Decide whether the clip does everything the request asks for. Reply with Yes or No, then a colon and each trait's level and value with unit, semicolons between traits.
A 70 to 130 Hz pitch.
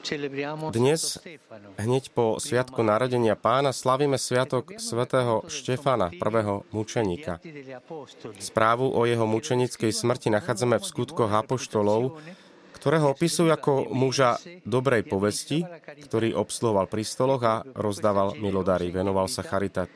Yes: low, 120 Hz